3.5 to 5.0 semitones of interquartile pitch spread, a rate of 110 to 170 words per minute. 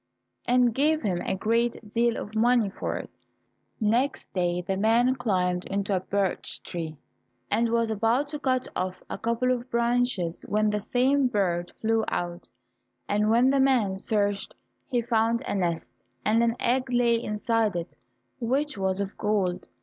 Yes: average, 3.9 semitones; average, 165 wpm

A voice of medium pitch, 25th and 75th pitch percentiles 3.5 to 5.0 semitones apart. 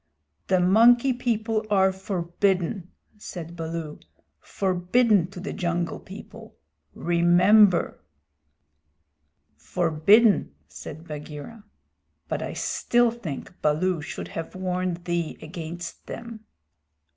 Yes: medium, 180 Hz; average, 3.9 semitones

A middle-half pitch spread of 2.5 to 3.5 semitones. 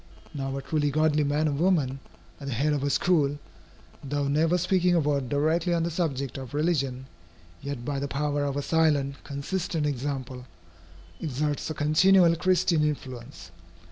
Yes: average, 2.8 semitones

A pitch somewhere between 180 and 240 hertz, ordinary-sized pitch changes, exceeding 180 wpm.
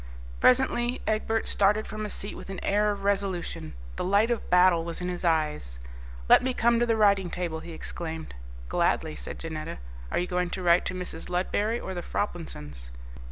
Yes: medium, 185 Hz; average, 3.9 semitones; average, 190 wpm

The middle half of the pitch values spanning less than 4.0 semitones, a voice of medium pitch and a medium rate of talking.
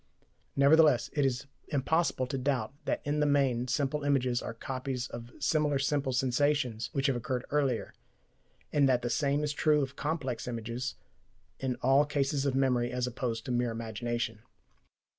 No: average, 2.8 semitones; low, 130 Hz; average, 160 wpm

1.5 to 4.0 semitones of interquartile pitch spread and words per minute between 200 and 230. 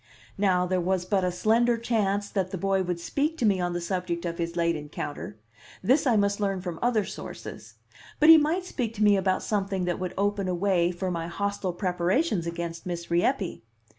Yes: average, 3.0 semitones; fast, 205 wpm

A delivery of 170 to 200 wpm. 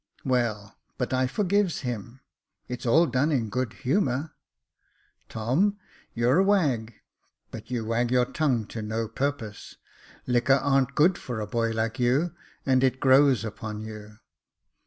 No: average, 145 wpm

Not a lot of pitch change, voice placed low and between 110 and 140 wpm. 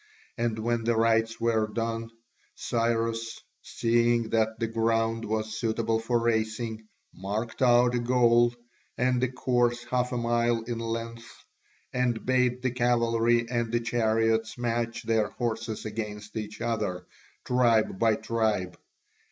Yes: narrow, 1.2 semitones; low, 115 Hz; slow, 135 wpm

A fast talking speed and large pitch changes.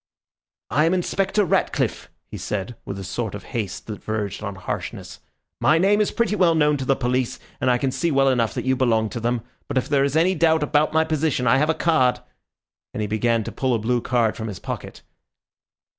Yes: fast, 220 wpm; wide, 5.9 semitones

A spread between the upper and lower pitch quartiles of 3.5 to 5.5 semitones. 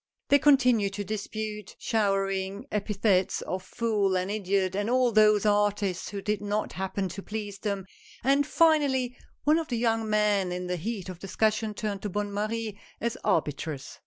No: narrow, 2.5 semitones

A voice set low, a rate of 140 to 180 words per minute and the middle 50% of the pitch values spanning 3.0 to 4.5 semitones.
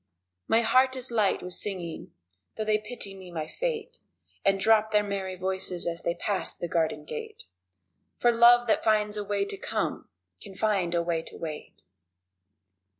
No: high, 200 Hz; average, 170 wpm; average, 4.0 semitones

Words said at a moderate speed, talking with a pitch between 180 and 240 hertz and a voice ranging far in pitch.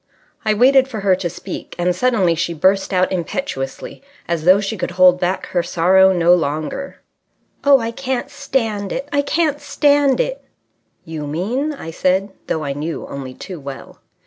Yes: average, 170 wpm; high, 190 Hz; wide, 7.1 semitones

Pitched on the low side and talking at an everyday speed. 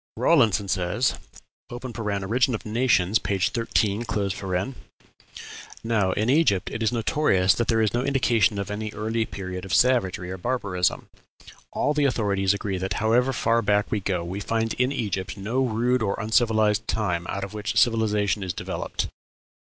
Yes: low, 105 Hz; average, 155 wpm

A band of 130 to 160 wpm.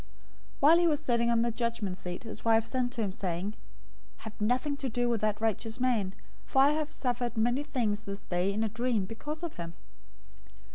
No: fast, 205 wpm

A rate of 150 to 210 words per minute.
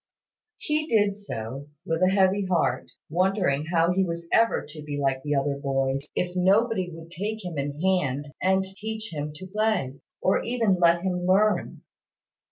Yes: average, 170 wpm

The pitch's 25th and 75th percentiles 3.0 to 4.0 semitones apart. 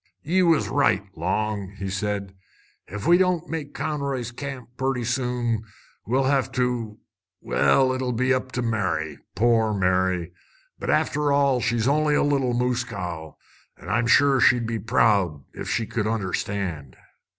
No: average, 4.7 semitones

